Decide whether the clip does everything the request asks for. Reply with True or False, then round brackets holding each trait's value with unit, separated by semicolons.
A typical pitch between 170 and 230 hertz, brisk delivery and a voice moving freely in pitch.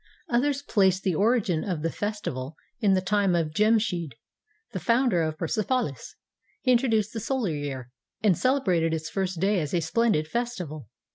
False (190 Hz; 165 wpm; 6.0 semitones)